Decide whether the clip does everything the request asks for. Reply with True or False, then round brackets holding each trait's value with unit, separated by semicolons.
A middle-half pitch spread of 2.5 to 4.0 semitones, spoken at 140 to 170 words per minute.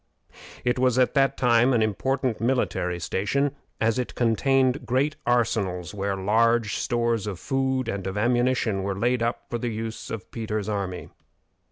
True (3.5 semitones; 160 wpm)